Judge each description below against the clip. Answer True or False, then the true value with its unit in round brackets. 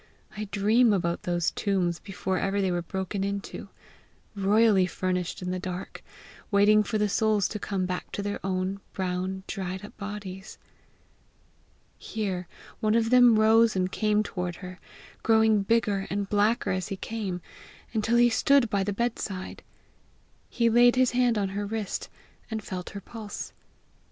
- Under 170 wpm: True (155 wpm)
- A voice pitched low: False (200 Hz)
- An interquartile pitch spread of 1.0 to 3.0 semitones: True (2.7 semitones)